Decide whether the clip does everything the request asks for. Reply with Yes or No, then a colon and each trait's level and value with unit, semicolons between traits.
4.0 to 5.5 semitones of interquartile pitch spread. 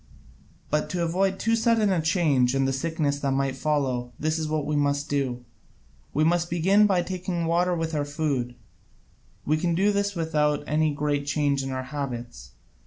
No: average, 3.6 semitones